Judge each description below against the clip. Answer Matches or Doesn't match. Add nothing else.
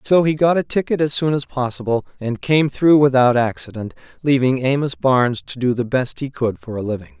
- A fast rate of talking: Matches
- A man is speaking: Matches